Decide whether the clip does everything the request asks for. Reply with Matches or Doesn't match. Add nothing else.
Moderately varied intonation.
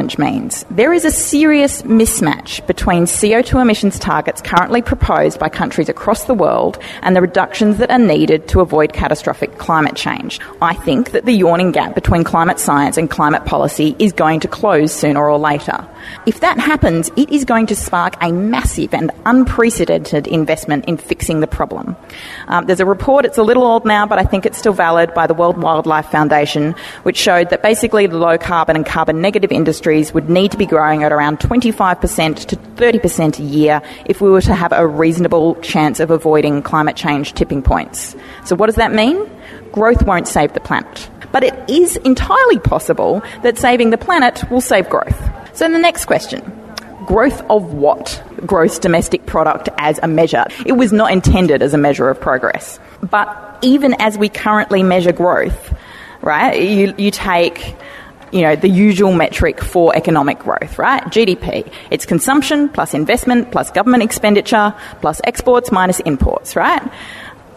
Doesn't match